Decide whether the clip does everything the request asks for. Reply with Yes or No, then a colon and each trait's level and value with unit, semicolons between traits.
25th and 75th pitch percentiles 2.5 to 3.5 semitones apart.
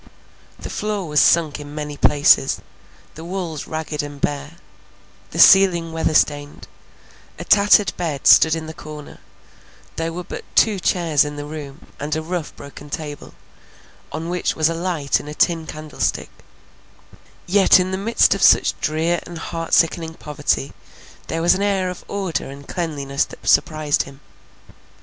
Yes: average, 2.9 semitones